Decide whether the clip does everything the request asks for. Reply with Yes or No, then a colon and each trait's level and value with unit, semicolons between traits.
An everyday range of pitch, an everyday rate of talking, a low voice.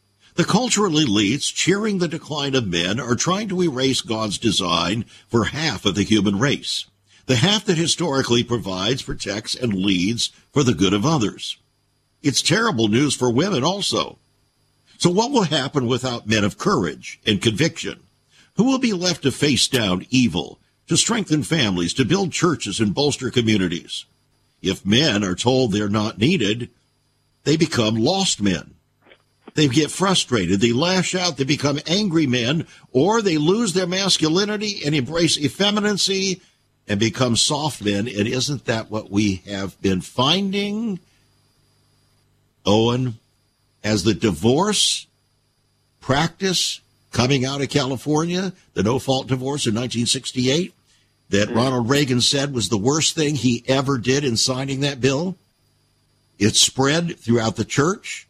No: wide, 6.6 semitones; average, 145 wpm; low, 130 Hz